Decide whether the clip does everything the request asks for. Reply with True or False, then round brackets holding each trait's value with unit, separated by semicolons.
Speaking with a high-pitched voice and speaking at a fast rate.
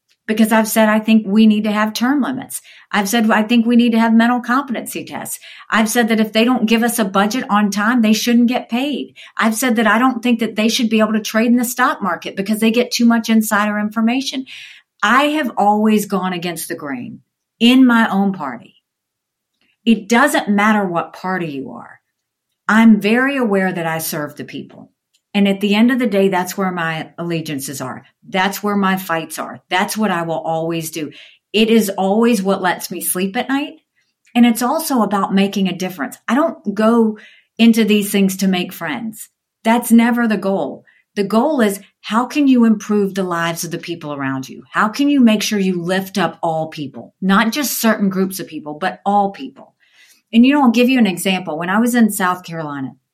True (210 Hz; 210 wpm)